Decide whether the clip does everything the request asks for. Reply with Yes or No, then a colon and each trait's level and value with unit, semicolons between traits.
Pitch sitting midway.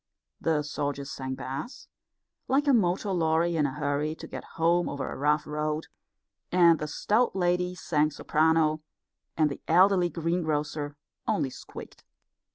Yes: medium, 160 Hz